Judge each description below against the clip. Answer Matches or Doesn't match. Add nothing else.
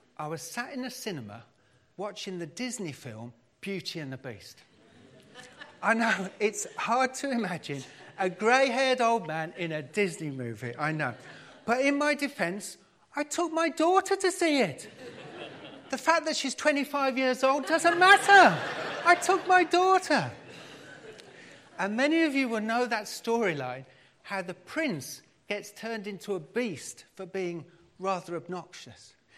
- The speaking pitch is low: Doesn't match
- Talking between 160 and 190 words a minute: Doesn't match